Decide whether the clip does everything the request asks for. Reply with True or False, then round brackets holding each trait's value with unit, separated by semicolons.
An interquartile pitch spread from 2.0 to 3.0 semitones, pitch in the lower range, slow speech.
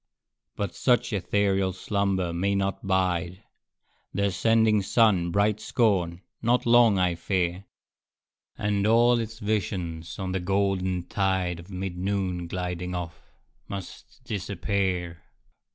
True (2.4 semitones; 95 Hz; 120 wpm)